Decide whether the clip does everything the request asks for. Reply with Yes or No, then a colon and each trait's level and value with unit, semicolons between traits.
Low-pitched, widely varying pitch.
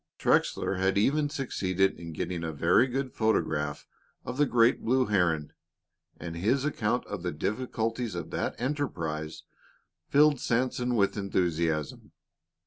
Yes: low, 105 Hz; wide, 7.0 semitones